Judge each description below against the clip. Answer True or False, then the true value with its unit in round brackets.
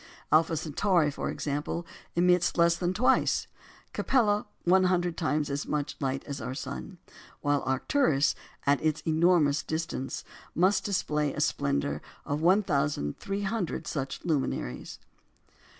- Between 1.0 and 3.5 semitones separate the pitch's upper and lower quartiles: False (4.1 semitones)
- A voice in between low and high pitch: True (155 Hz)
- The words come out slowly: True (120 wpm)